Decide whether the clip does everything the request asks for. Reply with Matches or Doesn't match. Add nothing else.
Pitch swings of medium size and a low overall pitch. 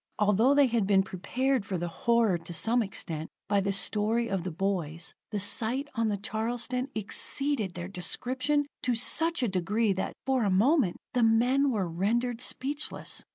Doesn't match